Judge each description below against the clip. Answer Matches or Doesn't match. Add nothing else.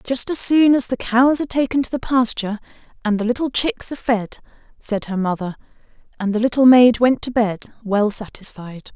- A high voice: Matches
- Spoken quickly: Doesn't match